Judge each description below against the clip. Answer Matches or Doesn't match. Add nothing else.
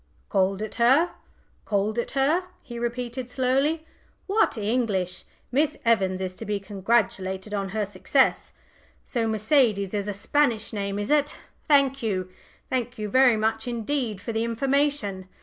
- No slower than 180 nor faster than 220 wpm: Doesn't match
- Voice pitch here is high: Matches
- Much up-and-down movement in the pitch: Doesn't match